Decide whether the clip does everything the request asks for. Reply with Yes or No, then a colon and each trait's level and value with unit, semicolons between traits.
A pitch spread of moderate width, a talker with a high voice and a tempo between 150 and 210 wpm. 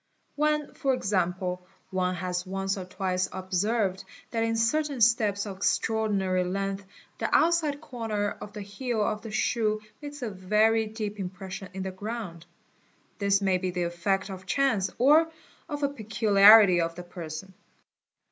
Yes: average, 3.3 semitones; high, 200 Hz; average, 155 wpm